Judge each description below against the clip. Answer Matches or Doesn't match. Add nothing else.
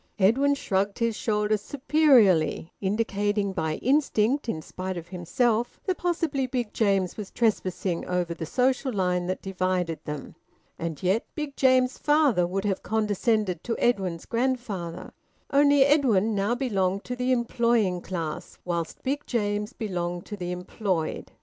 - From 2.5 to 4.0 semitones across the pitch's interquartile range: Doesn't match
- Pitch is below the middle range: Doesn't match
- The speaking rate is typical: Matches